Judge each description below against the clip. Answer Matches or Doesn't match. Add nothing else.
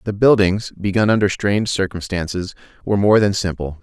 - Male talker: Matches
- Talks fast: Doesn't match